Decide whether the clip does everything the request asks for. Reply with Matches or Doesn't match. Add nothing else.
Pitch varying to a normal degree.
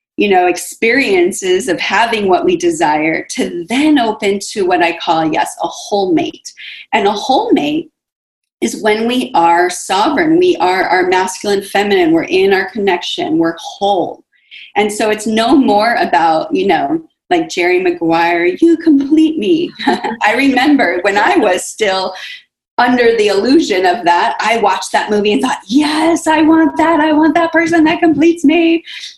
Doesn't match